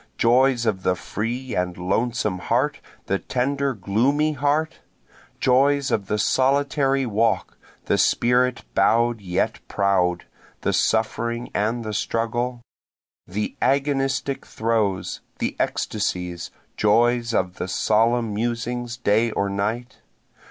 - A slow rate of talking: Yes, slow, 115 wpm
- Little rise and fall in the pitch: No, average, 3.7 semitones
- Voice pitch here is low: Yes, low, 115 Hz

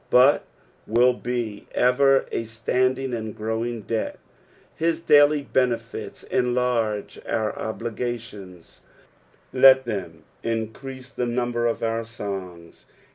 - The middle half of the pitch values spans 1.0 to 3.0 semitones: Yes, narrow, 2.5 semitones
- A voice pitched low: Yes, low, 120 Hz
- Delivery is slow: Yes, slow, 105 wpm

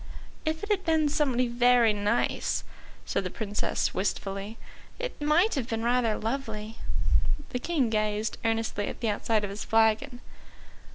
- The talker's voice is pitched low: No, high, 230 Hz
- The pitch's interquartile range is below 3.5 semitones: No, average, 4.3 semitones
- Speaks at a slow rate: No, average, 150 wpm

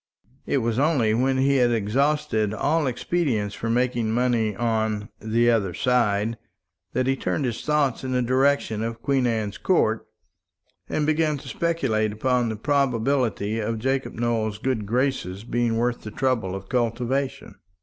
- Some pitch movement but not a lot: Yes, average, 3.4 semitones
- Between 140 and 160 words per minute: Yes, average, 155 wpm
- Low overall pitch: Yes, low, 120 Hz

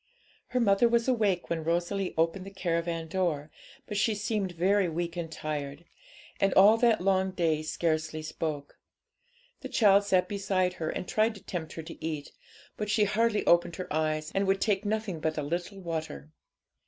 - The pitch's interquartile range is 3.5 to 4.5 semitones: Yes, average, 3.9 semitones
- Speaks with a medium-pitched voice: Yes, medium, 180 Hz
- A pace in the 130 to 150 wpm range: No, average, 180 wpm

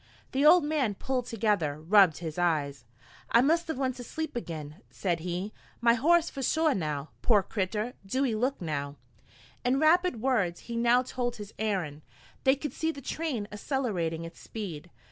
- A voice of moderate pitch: No, high, 225 Hz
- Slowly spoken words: No, average, 170 wpm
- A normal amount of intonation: No, wide, 7.5 semitones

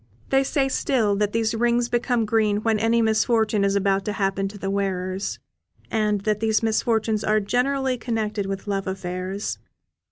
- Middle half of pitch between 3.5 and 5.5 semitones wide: No, narrow, 2.5 semitones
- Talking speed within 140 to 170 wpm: Yes, average, 165 wpm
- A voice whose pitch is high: Yes, high, 215 Hz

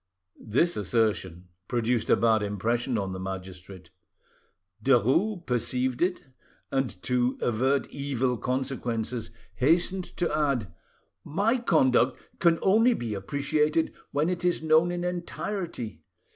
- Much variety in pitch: Yes, wide, 6.8 semitones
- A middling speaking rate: No, slow, 115 wpm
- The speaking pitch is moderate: No, low, 130 Hz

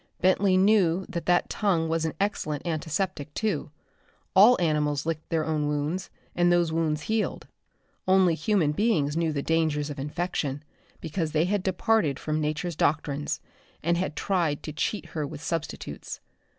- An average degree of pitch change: Yes, average, 3.5 semitones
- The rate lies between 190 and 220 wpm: No, average, 155 wpm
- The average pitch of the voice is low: No, medium, 165 Hz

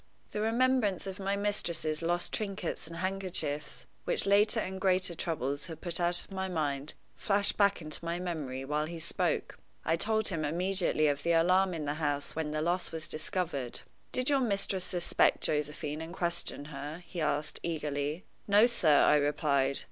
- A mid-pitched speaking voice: Yes, medium, 170 Hz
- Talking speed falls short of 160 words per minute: No, average, 175 wpm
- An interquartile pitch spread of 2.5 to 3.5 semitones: No, average, 4.1 semitones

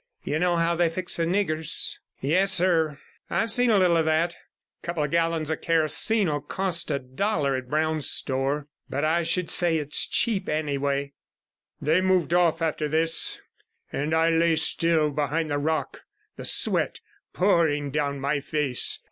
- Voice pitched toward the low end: No, medium, 160 Hz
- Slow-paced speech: No, average, 165 wpm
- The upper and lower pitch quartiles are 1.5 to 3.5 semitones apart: Yes, narrow, 2.6 semitones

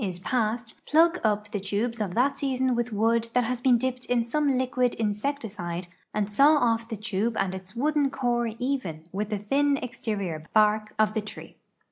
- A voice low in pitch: No, high, 230 Hz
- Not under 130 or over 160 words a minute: No, average, 190 wpm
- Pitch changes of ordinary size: Yes, average, 3.5 semitones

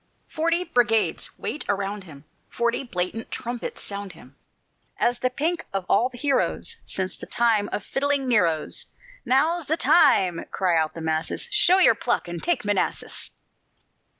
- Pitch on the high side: Yes, high, 230 Hz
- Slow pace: No, average, 150 wpm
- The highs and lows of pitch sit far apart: Yes, wide, 7.3 semitones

